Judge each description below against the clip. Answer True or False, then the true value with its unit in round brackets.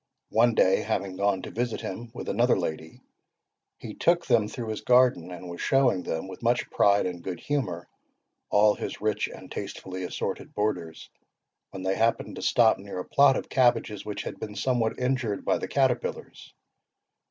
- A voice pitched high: False (105 Hz)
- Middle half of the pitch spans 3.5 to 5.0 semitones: True (4.4 semitones)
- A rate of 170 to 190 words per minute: True (175 wpm)